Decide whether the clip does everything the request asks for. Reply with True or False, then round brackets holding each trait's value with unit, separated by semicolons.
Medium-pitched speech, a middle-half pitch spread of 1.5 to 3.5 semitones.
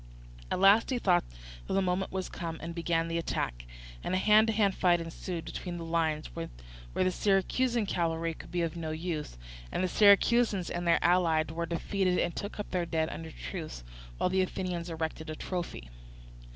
True (175 Hz; 2.6 semitones)